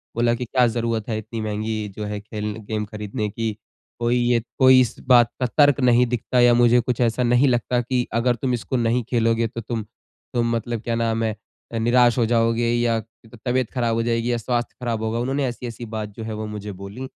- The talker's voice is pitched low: Yes, low, 115 Hz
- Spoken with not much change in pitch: Yes, narrow, 1.7 semitones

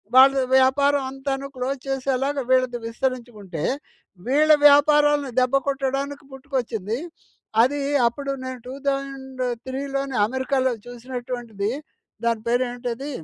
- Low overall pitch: No, very high, 265 Hz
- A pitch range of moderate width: No, narrow, 2.0 semitones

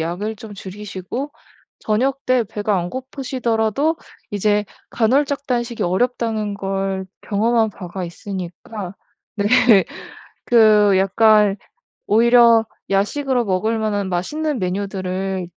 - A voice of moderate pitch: No, high, 210 Hz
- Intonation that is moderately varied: Yes, average, 3.6 semitones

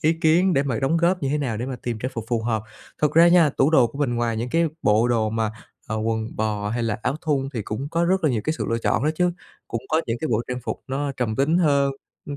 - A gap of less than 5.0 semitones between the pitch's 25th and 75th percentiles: No, average, 5.3 semitones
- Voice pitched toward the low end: Yes, low, 130 Hz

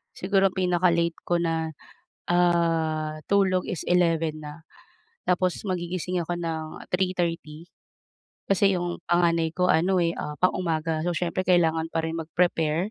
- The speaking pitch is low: No, medium, 170 Hz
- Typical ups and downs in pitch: No, narrow, 1.9 semitones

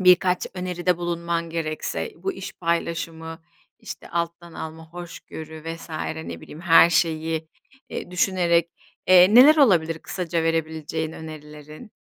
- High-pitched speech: No, medium, 170 Hz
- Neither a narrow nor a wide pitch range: No, narrow, 1.8 semitones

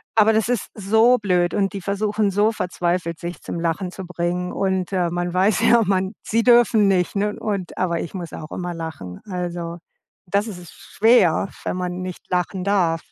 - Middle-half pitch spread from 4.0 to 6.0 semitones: No, average, 2.9 semitones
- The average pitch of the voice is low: No, medium, 185 Hz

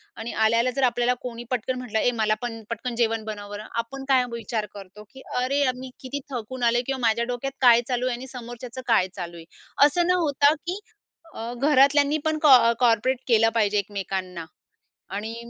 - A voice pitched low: No, high, 240 Hz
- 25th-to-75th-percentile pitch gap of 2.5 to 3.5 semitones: Yes, average, 3.0 semitones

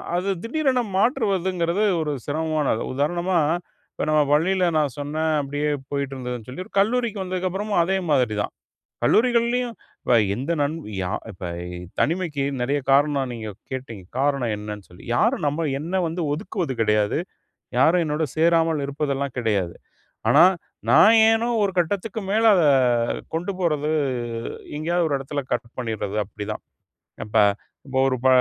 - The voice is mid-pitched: Yes, medium, 155 Hz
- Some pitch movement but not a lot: No, wide, 5.8 semitones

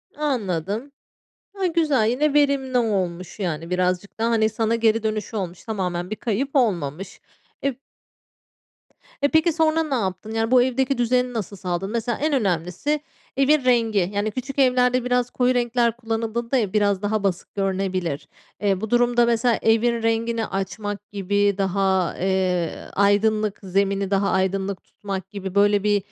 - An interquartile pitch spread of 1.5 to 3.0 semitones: No, average, 4.1 semitones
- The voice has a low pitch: No, high, 215 Hz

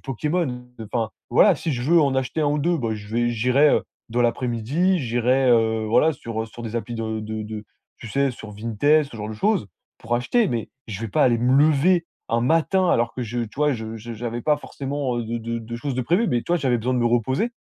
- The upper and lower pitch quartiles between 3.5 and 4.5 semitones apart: Yes, average, 4.2 semitones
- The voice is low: Yes, low, 120 Hz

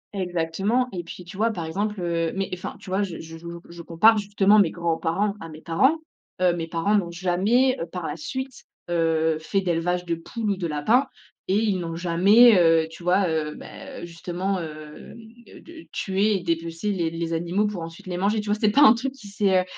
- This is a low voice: No, medium, 180 Hz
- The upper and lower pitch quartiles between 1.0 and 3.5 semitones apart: No, average, 3.9 semitones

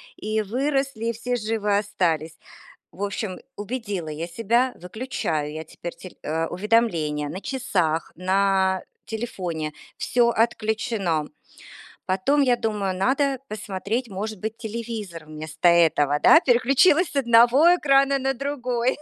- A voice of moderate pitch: No, high, 215 Hz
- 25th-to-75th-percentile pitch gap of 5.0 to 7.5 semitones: Yes, wide, 5.6 semitones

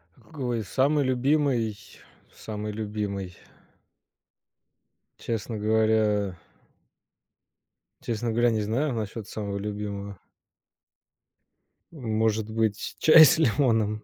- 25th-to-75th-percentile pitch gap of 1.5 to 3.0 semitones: Yes, narrow, 2.5 semitones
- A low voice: Yes, low, 110 Hz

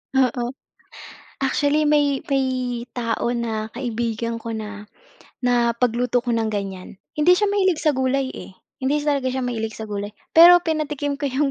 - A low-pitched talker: No, very high, 250 Hz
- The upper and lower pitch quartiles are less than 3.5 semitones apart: No, average, 4.2 semitones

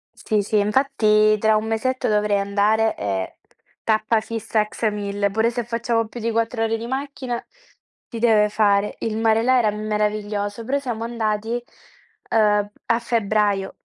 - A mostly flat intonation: Yes, narrow, 1.7 semitones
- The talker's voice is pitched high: Yes, high, 220 Hz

